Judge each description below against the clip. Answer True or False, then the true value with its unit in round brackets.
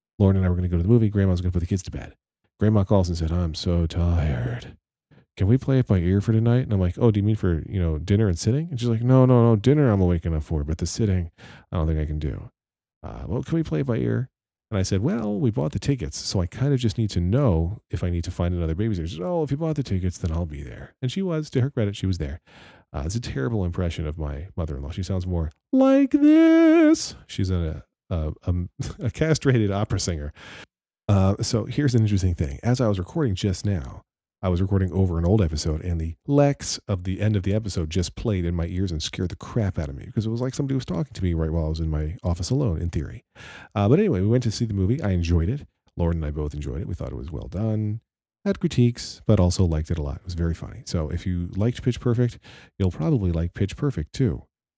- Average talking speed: False (270 wpm)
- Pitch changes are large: True (5.7 semitones)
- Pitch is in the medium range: False (95 Hz)